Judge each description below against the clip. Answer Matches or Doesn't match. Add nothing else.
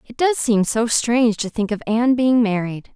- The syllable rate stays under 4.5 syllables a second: Doesn't match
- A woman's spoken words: Matches